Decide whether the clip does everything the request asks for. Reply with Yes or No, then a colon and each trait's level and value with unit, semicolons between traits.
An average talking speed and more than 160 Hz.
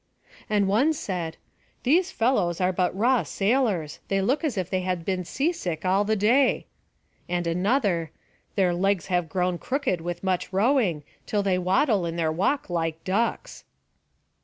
Yes: average, 160 wpm; high, 190 Hz